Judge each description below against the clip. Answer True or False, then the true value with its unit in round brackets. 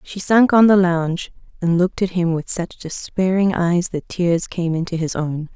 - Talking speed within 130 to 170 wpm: False (205 wpm)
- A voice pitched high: False (175 Hz)